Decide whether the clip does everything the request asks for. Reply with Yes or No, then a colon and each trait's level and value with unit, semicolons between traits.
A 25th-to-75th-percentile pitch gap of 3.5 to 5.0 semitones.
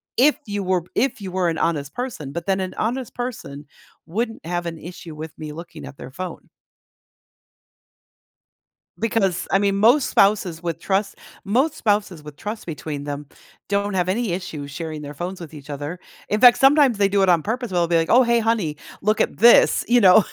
No: wide, 5.4 semitones